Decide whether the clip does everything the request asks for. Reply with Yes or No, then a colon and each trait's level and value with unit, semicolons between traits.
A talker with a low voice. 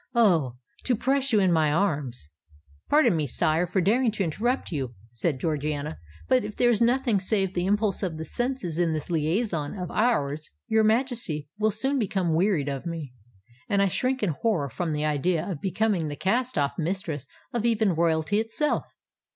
No: medium, 180 Hz